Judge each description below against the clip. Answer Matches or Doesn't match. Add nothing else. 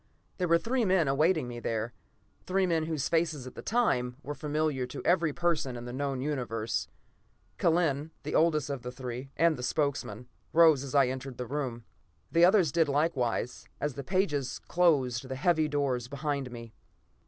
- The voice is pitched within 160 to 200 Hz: Doesn't match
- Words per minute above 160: Matches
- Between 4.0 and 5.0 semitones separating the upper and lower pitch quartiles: Matches